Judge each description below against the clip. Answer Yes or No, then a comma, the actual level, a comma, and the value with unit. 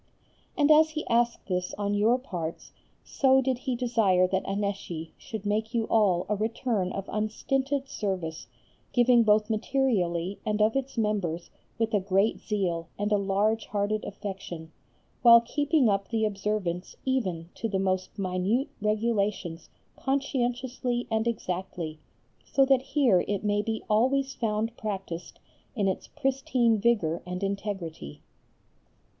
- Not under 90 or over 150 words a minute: Yes, average, 140 wpm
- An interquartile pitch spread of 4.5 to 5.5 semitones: No, average, 4.0 semitones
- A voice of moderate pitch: No, high, 210 Hz